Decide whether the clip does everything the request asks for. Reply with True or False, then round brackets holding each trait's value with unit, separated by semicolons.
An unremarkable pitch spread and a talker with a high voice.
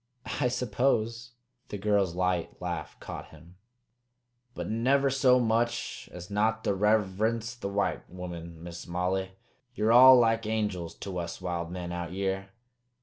False (4.3 semitones; 100 Hz)